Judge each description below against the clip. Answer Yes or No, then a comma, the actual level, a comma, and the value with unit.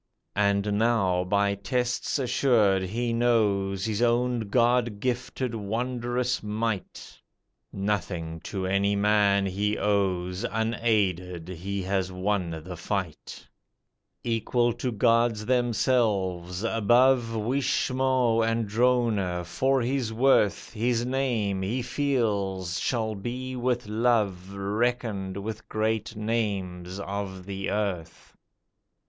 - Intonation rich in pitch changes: No, average, 3.6 semitones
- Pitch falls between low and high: No, low, 105 Hz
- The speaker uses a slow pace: Yes, slow, 105 wpm